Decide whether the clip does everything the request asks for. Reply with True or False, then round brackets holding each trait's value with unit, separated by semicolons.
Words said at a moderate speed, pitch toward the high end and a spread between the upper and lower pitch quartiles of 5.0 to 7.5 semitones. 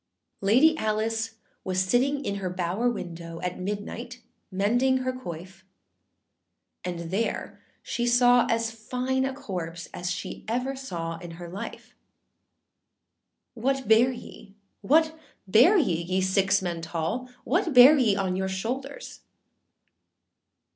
False (130 wpm; 215 Hz; 5.6 semitones)